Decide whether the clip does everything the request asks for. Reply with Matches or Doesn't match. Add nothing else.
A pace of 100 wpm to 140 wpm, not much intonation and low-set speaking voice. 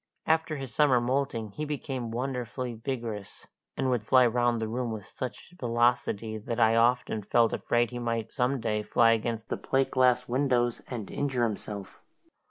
Doesn't match